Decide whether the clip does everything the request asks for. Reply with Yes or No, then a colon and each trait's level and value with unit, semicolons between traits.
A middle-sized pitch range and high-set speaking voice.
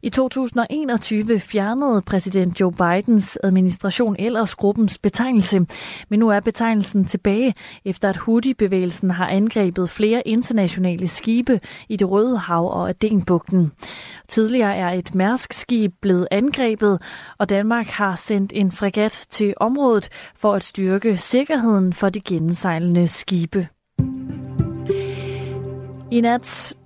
Yes: average, 3.7 semitones; high, 200 Hz